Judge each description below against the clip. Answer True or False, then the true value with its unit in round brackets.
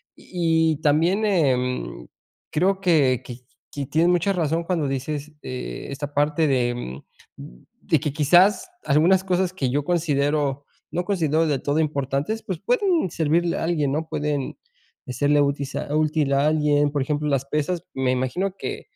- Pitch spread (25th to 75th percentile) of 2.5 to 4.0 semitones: True (3.6 semitones)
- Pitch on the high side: False (150 Hz)